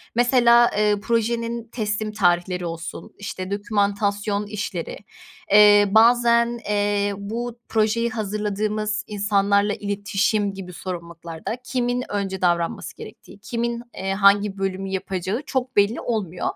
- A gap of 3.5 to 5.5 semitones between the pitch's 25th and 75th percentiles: No, average, 2.8 semitones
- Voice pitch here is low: No, high, 205 Hz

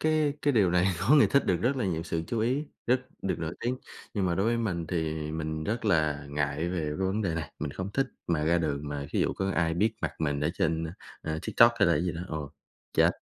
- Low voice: Yes, very low, 85 Hz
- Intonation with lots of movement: Yes, wide, 5.7 semitones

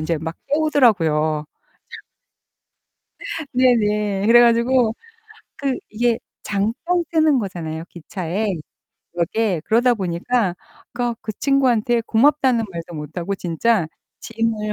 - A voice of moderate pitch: No, high, 220 Hz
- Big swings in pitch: Yes, wide, 5.7 semitones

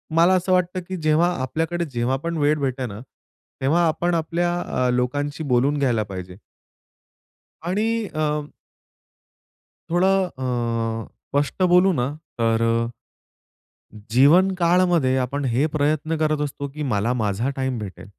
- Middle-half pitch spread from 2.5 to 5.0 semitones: No, wide, 5.5 semitones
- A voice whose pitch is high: No, medium, 145 Hz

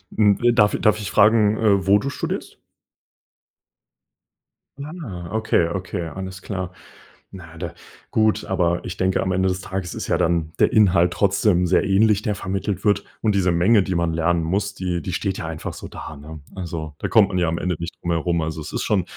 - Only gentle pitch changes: No, average, 3.0 semitones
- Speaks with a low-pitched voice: Yes, very low, 95 Hz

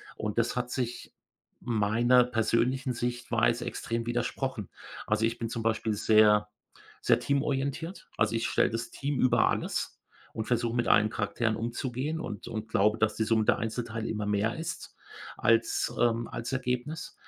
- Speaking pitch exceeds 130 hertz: No, low, 115 Hz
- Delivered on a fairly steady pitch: Yes, narrow, 2.1 semitones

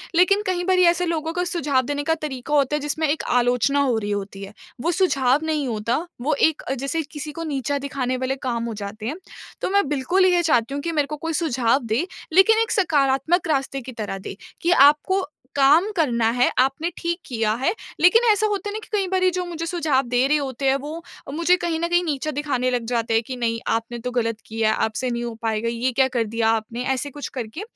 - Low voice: No, very high, 280 Hz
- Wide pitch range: Yes, wide, 5.7 semitones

